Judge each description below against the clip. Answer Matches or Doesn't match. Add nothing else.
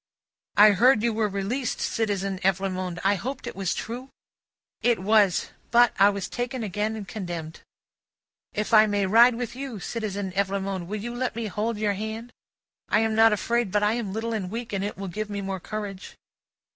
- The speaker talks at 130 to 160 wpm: Doesn't match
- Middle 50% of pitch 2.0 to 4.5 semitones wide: Matches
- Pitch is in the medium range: Doesn't match